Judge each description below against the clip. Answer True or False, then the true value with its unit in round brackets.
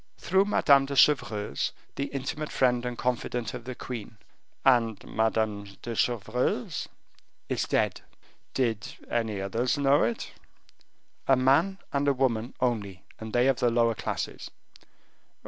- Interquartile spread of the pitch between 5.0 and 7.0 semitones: False (3.3 semitones)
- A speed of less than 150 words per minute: True (140 wpm)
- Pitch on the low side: True (120 Hz)